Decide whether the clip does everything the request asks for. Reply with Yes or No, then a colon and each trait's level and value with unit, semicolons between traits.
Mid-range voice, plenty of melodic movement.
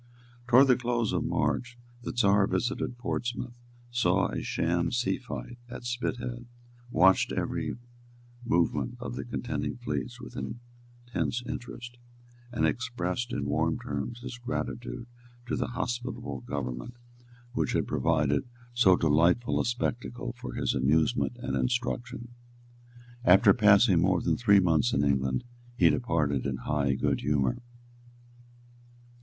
No: low, 120 Hz; wide, 6.6 semitones